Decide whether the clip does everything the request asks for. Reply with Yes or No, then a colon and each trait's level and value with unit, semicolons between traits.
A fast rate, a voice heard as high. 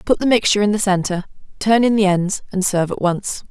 Yes: fast, 240 wpm; high, 200 Hz